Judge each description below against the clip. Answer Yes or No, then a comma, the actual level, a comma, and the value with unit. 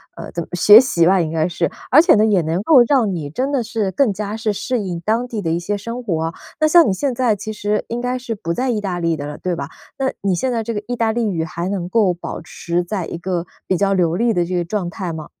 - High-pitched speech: Yes, high, 200 Hz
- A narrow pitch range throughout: No, average, 5.1 semitones